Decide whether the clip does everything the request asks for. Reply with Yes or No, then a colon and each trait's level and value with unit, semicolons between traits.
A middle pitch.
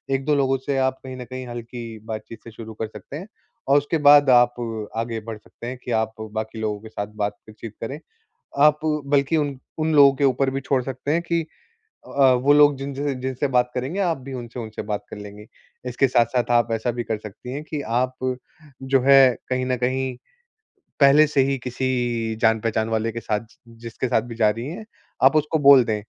No: low, 130 Hz